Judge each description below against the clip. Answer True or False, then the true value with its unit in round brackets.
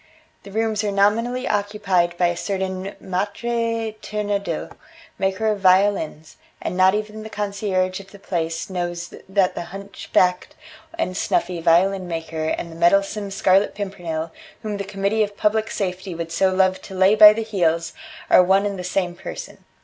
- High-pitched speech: True (195 Hz)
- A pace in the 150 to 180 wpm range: True (165 wpm)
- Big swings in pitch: False (2.5 semitones)